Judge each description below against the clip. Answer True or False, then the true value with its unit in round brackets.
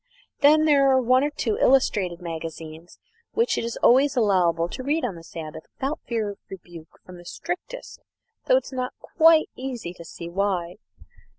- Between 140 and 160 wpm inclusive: False (180 wpm)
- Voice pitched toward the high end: True (220 Hz)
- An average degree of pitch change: False (8.1 semitones)